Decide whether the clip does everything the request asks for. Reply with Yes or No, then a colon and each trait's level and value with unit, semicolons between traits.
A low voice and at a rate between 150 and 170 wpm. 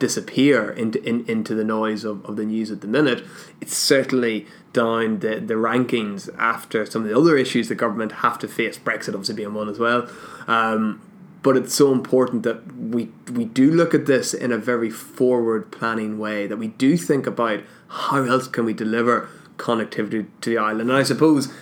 No: low, 115 Hz; average, 195 wpm